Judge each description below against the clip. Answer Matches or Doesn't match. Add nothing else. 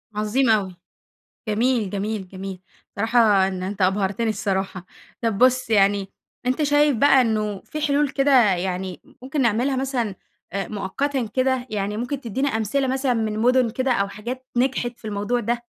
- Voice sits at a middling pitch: Doesn't match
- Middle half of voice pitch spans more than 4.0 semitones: Matches